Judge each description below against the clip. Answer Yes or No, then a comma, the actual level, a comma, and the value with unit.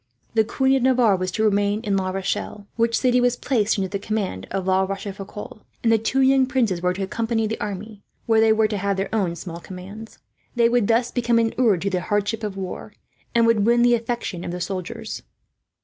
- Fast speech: Yes, fast, 210 wpm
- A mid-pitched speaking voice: No, high, 215 Hz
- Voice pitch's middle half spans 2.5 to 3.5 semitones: Yes, average, 3.2 semitones